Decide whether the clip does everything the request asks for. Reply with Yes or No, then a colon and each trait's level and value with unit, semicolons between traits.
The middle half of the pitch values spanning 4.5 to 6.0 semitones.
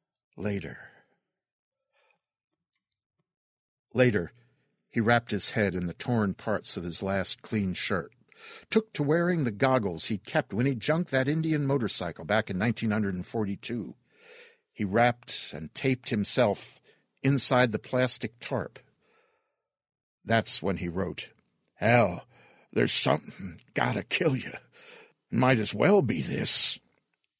Yes: average, 4.8 semitones